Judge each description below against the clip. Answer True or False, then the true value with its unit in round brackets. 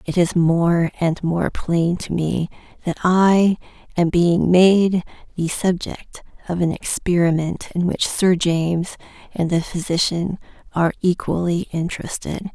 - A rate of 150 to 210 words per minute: False (135 wpm)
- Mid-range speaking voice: True (175 Hz)